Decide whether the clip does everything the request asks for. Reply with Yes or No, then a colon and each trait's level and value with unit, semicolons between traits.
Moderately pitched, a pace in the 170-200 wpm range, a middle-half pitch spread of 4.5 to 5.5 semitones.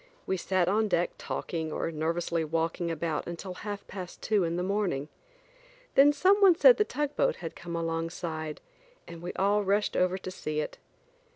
No: medium, 175 Hz; average, 175 wpm; average, 3.7 semitones